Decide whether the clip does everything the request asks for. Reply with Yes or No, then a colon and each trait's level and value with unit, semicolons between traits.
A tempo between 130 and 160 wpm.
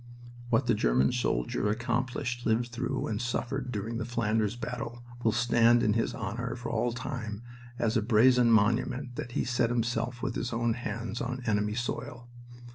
No: average, 170 wpm